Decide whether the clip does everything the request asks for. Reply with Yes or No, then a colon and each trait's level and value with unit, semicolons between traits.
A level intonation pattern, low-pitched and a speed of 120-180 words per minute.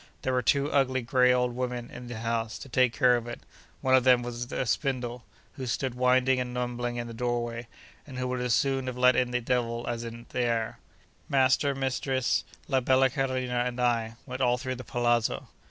No: narrow, 1.3 semitones; low, 125 Hz; fast, 205 wpm